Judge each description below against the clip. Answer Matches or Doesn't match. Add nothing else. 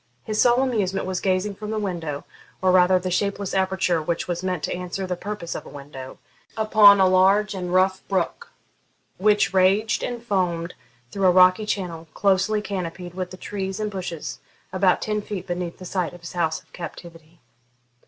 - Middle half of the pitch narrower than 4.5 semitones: Matches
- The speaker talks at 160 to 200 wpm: Matches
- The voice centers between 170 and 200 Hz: Matches